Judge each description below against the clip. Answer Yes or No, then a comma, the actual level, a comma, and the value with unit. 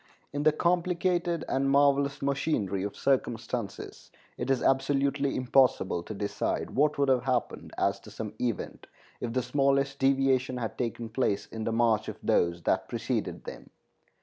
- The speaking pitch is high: No, low, 135 Hz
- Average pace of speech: Yes, average, 155 wpm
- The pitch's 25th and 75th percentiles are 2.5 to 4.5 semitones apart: Yes, average, 3.5 semitones